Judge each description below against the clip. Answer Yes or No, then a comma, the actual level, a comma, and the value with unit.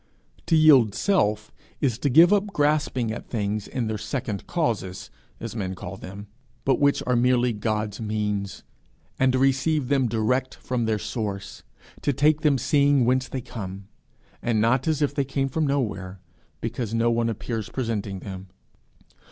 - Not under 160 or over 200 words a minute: Yes, average, 165 wpm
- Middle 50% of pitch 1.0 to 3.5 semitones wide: No, average, 4.4 semitones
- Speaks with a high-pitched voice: No, low, 120 Hz